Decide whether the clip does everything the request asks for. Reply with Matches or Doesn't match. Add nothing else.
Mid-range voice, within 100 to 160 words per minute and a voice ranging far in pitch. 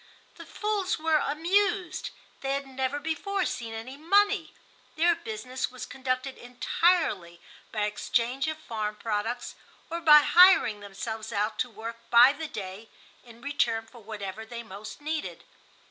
Doesn't match